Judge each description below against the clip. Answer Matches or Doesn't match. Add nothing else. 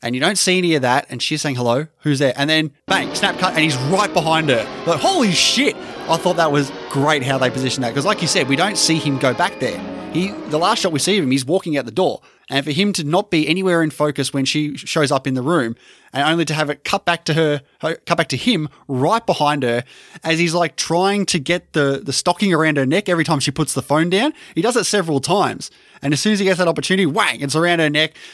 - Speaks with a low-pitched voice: Doesn't match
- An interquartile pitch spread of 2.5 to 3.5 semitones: Doesn't match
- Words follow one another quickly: Matches